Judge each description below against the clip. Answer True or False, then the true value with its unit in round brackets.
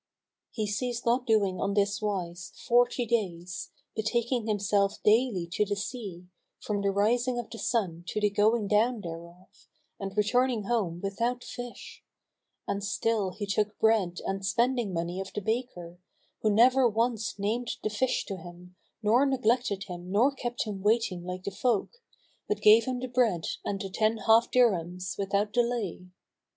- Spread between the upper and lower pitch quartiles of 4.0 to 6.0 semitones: False (3.6 semitones)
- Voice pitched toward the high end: True (210 Hz)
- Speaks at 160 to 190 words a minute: True (165 wpm)